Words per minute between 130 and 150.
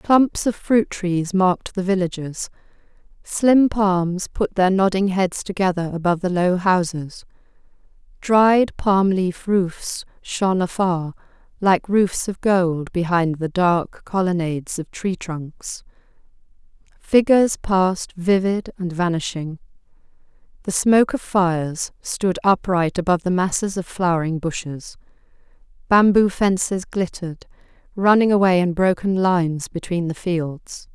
No: slow, 120 wpm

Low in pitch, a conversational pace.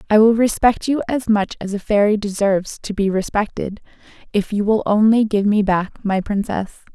No: high, 210 Hz; average, 190 wpm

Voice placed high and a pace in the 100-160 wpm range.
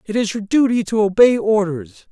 No: high, 210 Hz; average, 200 wpm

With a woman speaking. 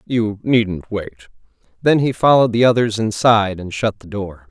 No: male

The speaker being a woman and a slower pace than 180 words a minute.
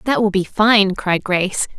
No: female; average, 200 wpm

